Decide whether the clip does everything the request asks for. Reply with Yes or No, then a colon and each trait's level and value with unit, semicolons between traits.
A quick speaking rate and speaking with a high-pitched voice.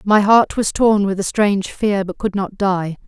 Yes: fast, 235 wpm; high, 200 Hz